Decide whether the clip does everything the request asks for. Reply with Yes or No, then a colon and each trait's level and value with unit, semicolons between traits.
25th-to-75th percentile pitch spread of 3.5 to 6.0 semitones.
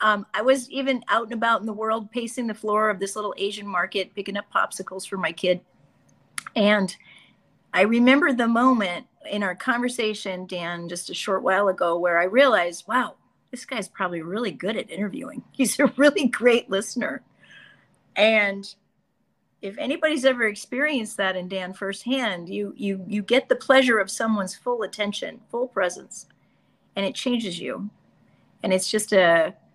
Yes: average, 4.1 semitones